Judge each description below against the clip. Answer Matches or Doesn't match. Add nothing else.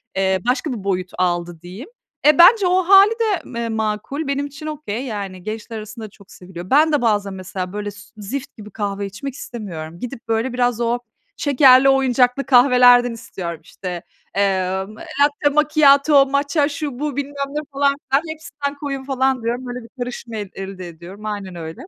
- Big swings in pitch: Matches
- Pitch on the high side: Matches